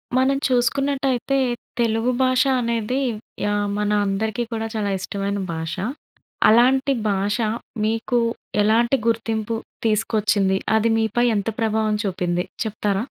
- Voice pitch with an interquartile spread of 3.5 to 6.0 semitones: No, average, 2.7 semitones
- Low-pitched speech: No, high, 220 Hz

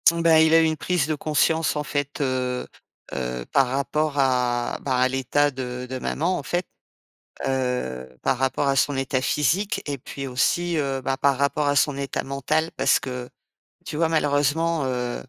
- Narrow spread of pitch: No, average, 3.2 semitones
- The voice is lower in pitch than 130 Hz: No, medium, 140 Hz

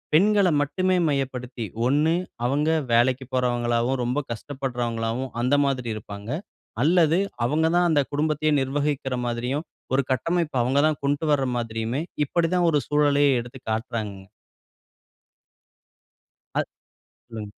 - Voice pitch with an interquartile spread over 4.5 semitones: No, average, 3.8 semitones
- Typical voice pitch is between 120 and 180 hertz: Yes, low, 135 Hz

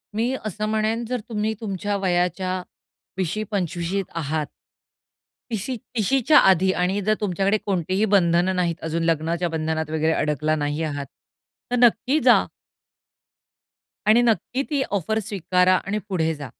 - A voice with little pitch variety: No, average, 4.6 semitones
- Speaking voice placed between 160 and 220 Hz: Yes, medium, 185 Hz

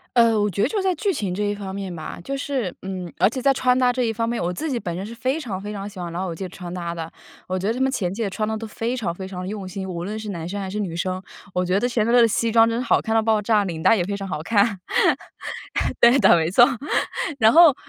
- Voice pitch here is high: Yes, high, 205 Hz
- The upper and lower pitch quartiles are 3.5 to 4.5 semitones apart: Yes, average, 4.1 semitones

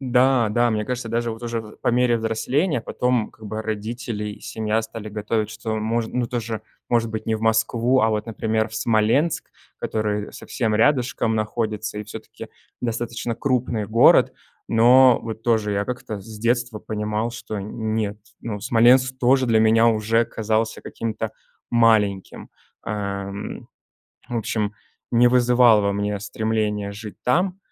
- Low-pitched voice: Yes, low, 110 Hz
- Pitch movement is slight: Yes, narrow, 1.8 semitones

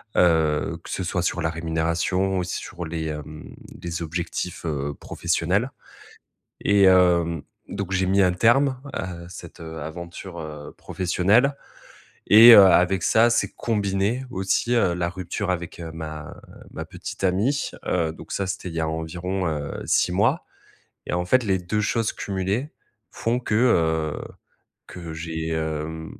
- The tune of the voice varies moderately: Yes, average, 3.2 semitones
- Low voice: Yes, very low, 90 Hz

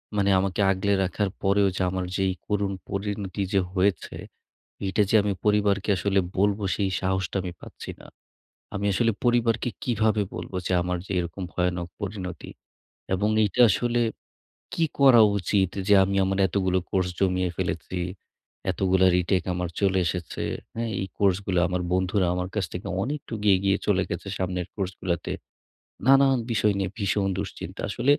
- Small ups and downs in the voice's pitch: Yes, narrow, 2.0 semitones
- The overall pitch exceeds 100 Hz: No, very low, 95 Hz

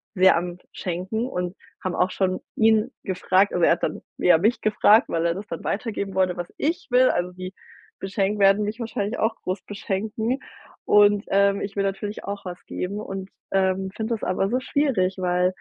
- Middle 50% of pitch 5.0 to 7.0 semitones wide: No, narrow, 2.6 semitones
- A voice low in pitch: No, high, 195 Hz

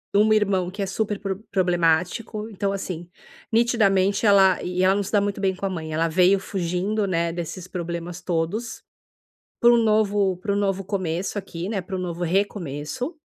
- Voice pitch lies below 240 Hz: Yes, high, 190 Hz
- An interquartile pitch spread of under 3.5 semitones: Yes, narrow, 2.6 semitones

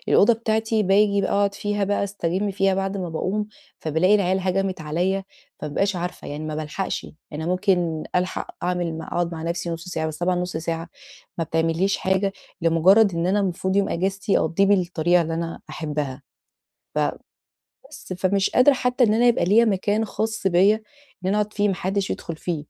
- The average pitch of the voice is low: No, medium, 185 Hz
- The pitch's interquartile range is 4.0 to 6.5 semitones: No, average, 3.2 semitones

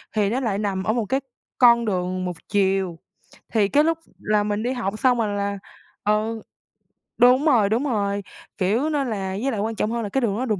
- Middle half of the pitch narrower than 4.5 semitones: Yes, average, 3.5 semitones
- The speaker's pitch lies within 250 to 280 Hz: No, high, 215 Hz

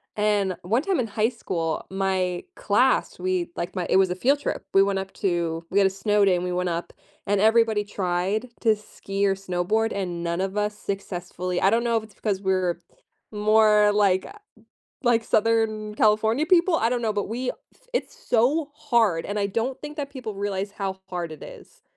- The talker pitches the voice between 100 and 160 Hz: No, high, 205 Hz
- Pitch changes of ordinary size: Yes, average, 3.3 semitones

